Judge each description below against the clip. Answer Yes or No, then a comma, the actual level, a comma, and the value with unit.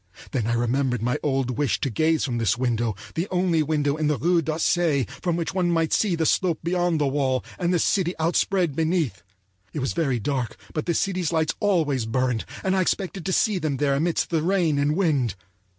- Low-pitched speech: No, medium, 155 Hz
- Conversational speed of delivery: No, fast, 210 wpm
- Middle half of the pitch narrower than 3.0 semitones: No, average, 4.6 semitones